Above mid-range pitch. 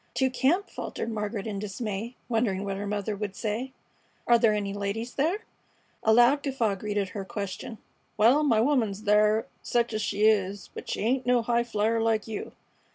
Yes: high, 220 Hz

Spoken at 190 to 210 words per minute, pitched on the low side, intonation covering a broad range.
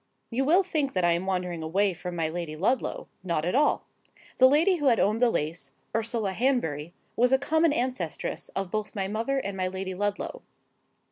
No: average, 195 wpm; high, 205 Hz; wide, 6.6 semitones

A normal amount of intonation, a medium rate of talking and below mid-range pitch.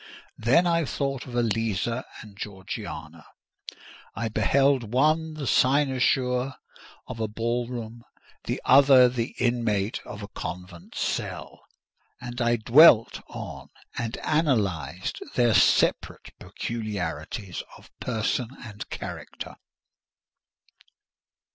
No: average, 3.3 semitones; slow, 105 wpm; low, 120 Hz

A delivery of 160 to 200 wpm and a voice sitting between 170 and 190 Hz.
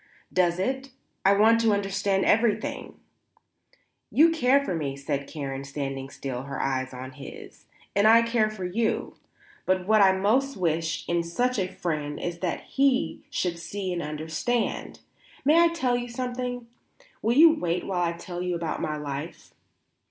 Yes: average, 165 wpm; medium, 185 Hz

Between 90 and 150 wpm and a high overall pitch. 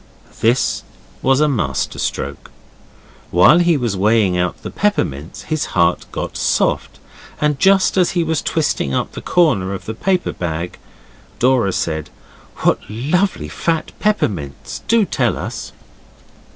No: average, 140 wpm; low, 125 Hz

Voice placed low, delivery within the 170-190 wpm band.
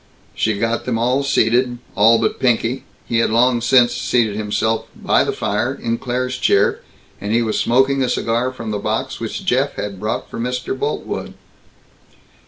Yes: low, 115 Hz; average, 175 wpm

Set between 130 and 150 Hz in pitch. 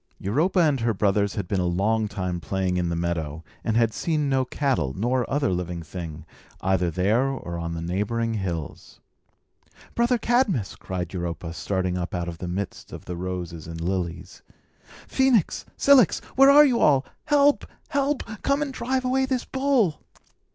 No: low, 100 Hz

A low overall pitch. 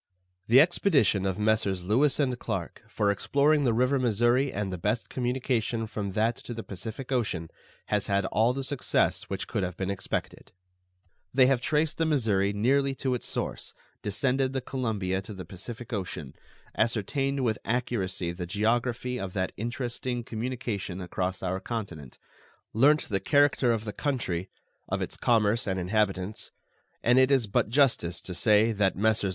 Yes: low, 110 Hz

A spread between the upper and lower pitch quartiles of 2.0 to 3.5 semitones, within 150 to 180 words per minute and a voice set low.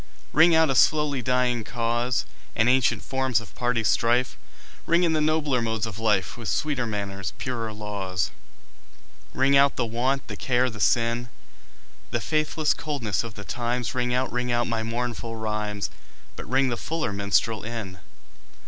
Yes: average, 2.9 semitones; average, 165 wpm; low, 120 Hz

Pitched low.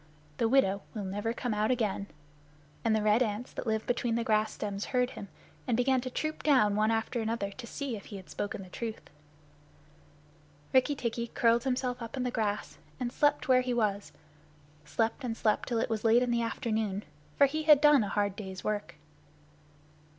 No: high, 230 Hz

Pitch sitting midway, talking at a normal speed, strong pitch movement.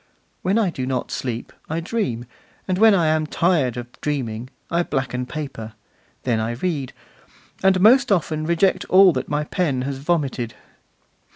Yes: medium, 150 Hz; average, 160 wpm; wide, 6.2 semitones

